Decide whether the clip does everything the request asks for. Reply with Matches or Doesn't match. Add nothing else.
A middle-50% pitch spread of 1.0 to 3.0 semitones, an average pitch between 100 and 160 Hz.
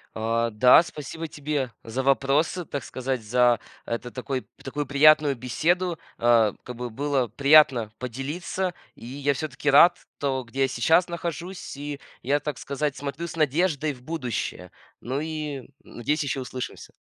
Doesn't match